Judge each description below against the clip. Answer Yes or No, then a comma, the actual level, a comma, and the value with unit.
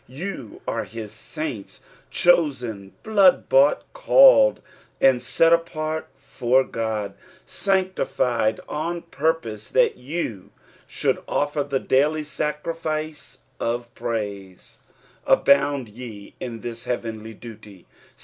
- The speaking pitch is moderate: No, low, 130 Hz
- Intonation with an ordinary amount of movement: No, wide, 5.9 semitones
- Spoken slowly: Yes, slow, 105 wpm